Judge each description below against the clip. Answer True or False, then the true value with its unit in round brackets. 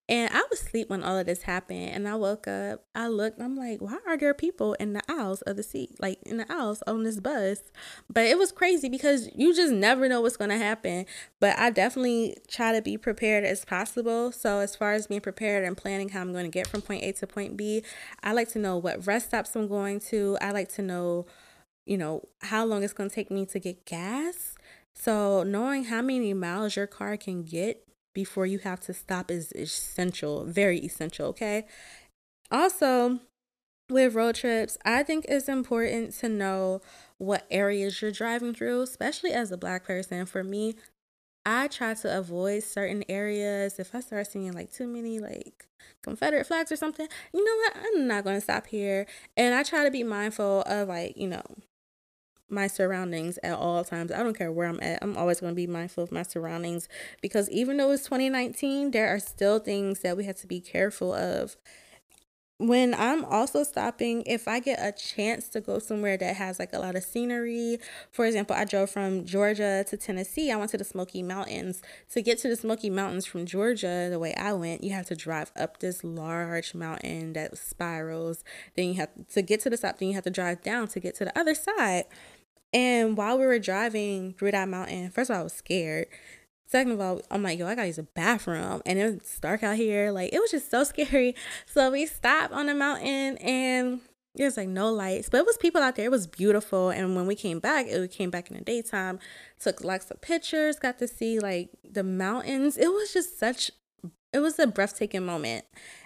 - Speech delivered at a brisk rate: True (210 wpm)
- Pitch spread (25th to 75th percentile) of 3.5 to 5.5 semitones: True (4.2 semitones)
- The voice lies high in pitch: True (205 Hz)